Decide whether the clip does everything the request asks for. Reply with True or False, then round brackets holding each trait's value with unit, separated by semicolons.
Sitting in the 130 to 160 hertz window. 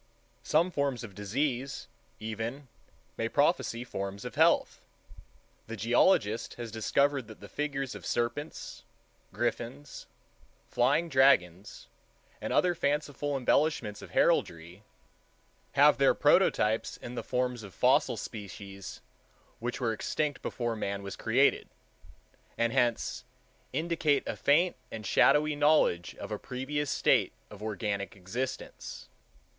False (120 Hz)